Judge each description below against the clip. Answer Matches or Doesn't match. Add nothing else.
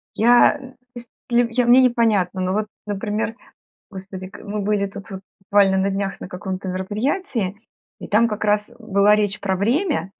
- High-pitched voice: Matches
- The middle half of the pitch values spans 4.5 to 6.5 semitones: Doesn't match